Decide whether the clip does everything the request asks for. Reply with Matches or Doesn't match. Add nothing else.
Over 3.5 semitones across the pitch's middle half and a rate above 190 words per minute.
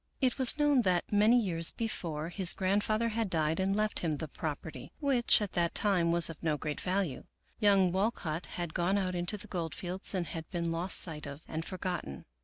Matches